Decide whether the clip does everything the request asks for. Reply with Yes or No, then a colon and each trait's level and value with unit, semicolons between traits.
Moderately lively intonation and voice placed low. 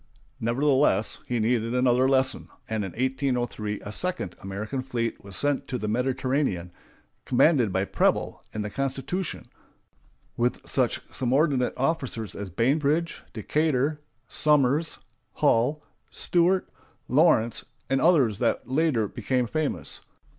Yes: average, 4.3 semitones; low, 130 Hz